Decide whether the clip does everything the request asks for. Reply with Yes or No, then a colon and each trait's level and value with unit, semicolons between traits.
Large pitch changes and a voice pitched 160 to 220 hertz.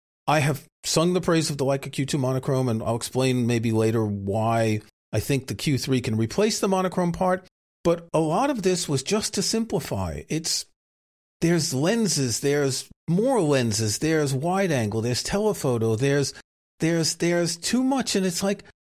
No: wide, 7.9 semitones; medium, 140 Hz